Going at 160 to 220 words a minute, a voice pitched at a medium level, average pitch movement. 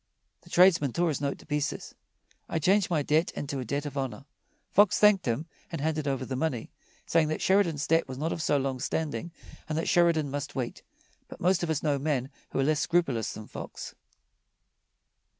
Yes: average, 200 wpm; medium, 150 Hz; average, 3.4 semitones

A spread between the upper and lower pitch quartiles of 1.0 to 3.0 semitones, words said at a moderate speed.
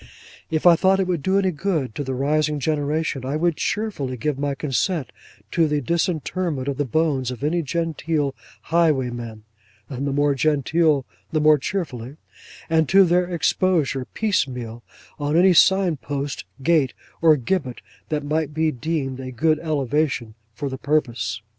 No: average, 3.7 semitones; average, 155 wpm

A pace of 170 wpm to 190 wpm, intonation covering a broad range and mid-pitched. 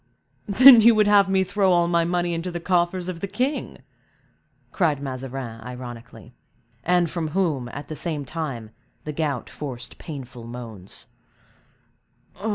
No: average, 145 wpm; wide, 6.1 semitones; medium, 165 Hz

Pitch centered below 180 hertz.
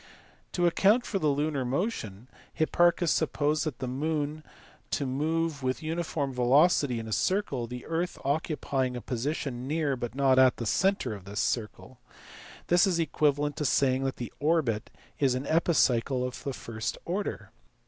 Yes: medium, 140 Hz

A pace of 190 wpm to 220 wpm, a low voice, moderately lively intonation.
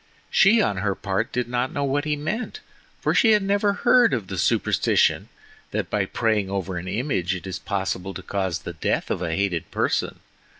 No: average, 200 wpm; low, 105 Hz; wide, 8.0 semitones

